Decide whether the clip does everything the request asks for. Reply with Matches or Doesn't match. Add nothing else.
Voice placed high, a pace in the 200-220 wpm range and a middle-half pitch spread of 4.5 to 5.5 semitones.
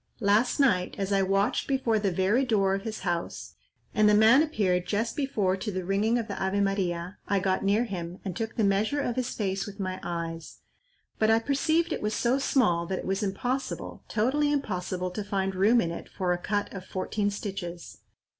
Doesn't match